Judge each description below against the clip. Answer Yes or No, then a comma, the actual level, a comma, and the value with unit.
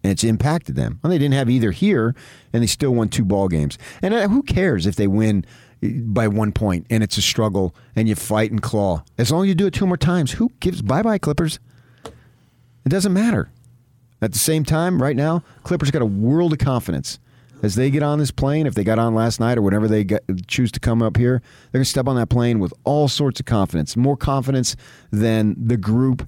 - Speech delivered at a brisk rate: Yes, fast, 235 wpm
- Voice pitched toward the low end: Yes, low, 120 Hz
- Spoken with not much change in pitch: No, average, 4.6 semitones